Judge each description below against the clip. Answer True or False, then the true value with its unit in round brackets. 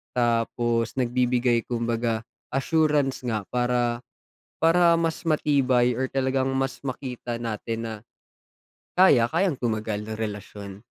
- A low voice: True (125 Hz)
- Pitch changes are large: False (2.7 semitones)